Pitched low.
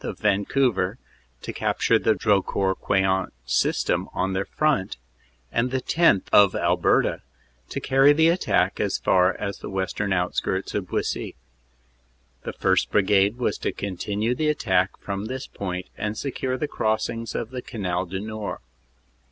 Yes: low, 100 Hz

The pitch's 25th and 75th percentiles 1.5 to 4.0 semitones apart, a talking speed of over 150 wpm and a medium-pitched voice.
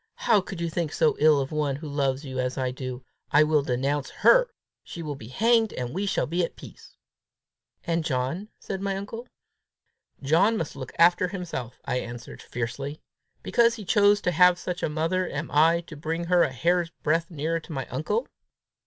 No: average, 4.7 semitones; average, 195 wpm; medium, 160 Hz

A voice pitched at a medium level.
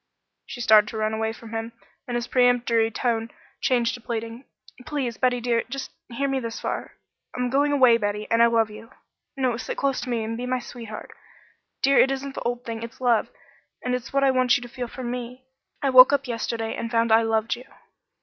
No: high, 240 Hz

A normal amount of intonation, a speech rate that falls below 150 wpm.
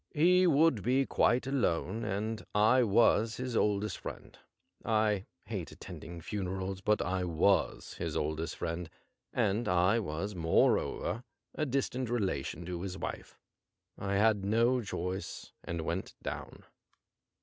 Yes: average, 4.6 semitones; average, 140 wpm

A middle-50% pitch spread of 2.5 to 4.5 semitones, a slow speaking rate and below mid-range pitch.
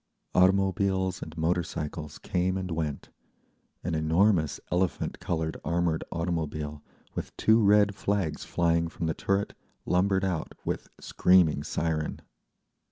Yes: average, 3.0 semitones; slow, 115 wpm; very low, 85 Hz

